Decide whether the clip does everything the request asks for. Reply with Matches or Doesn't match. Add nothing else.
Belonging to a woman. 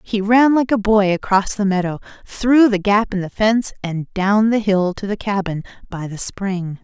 Matches